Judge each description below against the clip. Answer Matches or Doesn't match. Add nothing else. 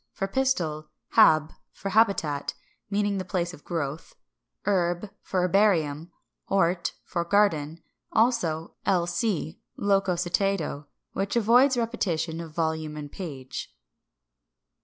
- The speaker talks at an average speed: Doesn't match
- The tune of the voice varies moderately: Matches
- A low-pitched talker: Doesn't match